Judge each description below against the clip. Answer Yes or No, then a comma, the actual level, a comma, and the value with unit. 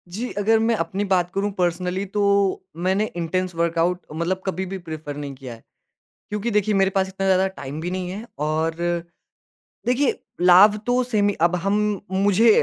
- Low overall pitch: No, high, 190 Hz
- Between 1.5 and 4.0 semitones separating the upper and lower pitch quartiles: Yes, average, 3.1 semitones